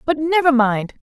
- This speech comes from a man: No, female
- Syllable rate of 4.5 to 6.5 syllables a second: Yes, 4.9 syllables/s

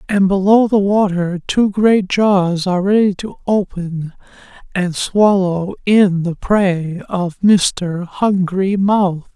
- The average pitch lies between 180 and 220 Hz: Yes, high, 190 Hz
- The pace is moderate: No, slow, 130 wpm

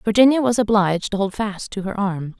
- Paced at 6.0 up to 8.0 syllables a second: No, 5.7 syllables/s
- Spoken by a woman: Yes, female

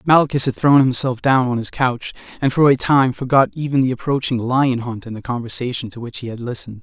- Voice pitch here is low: Yes, low, 125 Hz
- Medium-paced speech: No, fast, 230 wpm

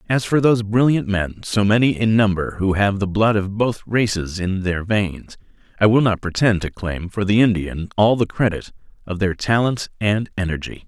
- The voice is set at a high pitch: No, low, 100 Hz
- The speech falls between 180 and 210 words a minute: Yes, average, 200 wpm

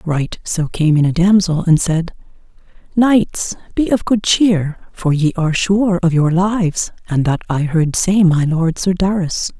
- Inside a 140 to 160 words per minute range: No, average, 180 wpm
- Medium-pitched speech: Yes, medium, 175 Hz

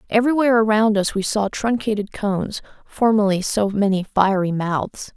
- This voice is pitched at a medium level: No, high, 210 Hz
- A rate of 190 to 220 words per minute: No, average, 140 wpm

